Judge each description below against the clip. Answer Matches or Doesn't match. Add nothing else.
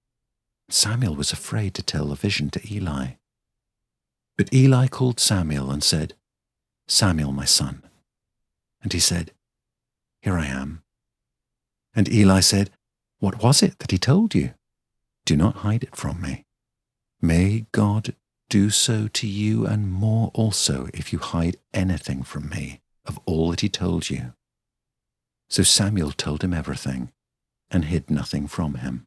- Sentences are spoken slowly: Doesn't match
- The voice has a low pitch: Matches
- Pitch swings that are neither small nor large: Doesn't match